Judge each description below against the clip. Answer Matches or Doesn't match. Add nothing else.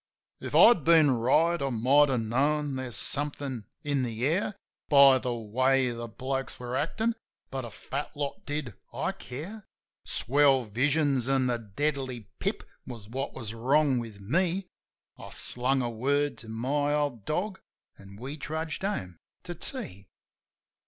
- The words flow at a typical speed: Matches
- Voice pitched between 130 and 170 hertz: Matches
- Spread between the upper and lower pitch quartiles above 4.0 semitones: Doesn't match